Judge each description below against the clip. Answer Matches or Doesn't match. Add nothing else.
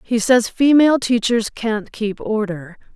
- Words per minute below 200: Matches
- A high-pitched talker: Matches